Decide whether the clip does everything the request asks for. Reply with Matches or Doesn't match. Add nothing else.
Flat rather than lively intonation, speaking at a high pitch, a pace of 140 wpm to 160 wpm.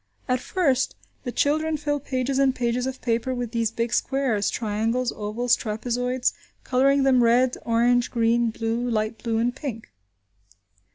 Matches